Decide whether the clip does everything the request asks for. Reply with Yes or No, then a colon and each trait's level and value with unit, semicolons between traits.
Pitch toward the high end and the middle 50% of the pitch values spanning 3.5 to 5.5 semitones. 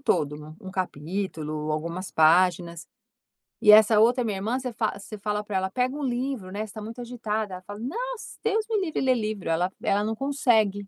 Yes: high, 210 Hz; average, 4.9 semitones